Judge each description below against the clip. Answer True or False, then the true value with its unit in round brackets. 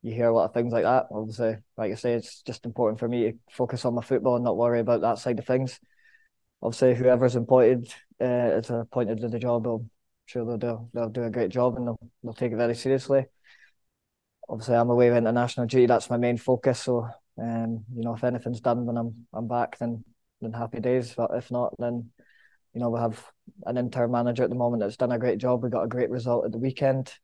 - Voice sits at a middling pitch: False (120 Hz)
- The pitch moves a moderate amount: False (1.1 semitones)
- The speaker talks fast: True (240 wpm)